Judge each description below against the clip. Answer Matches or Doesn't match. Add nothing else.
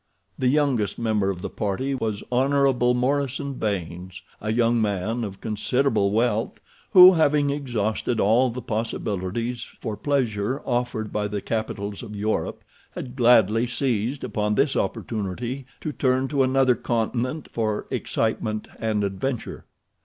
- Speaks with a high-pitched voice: Doesn't match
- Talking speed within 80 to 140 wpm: Matches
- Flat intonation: Doesn't match